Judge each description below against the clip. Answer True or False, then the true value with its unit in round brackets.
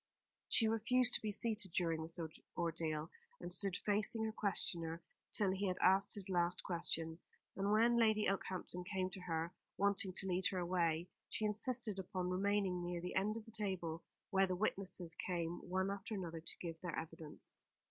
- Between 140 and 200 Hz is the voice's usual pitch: True (185 Hz)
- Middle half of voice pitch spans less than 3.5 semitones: True (3.1 semitones)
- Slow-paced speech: False (180 wpm)